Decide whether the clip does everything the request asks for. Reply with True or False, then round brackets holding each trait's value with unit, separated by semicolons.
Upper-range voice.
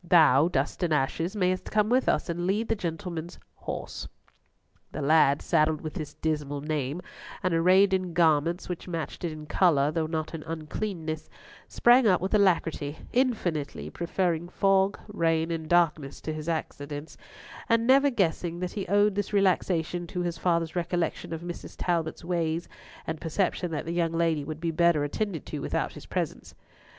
False (170 Hz)